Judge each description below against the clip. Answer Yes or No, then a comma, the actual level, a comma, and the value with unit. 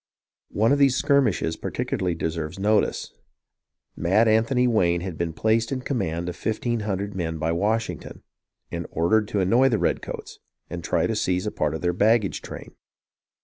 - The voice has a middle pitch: No, low, 100 Hz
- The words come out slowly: No, average, 175 wpm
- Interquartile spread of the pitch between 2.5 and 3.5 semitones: No, average, 4.8 semitones